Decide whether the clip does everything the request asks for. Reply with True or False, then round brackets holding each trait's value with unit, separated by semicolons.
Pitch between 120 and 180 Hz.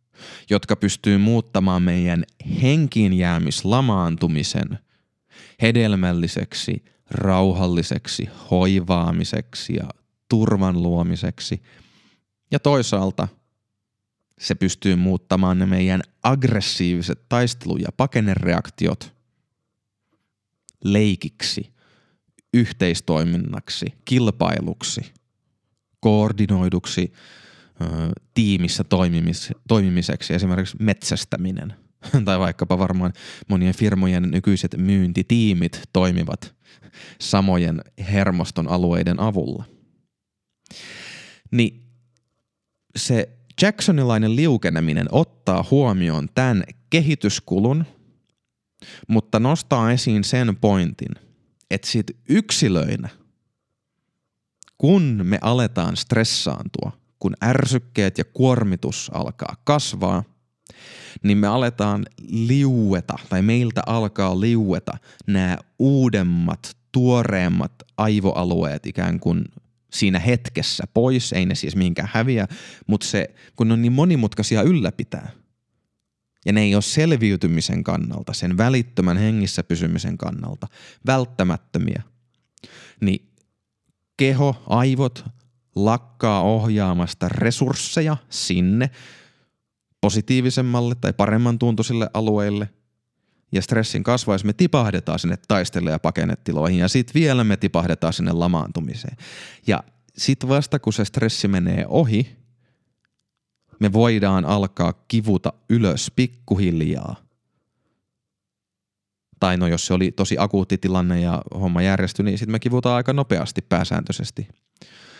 False (105 Hz)